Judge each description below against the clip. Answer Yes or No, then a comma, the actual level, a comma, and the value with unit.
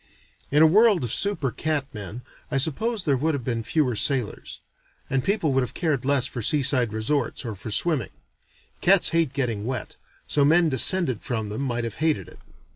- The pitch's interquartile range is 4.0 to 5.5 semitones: Yes, average, 4.9 semitones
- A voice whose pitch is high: No, low, 135 Hz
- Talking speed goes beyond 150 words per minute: Yes, average, 190 wpm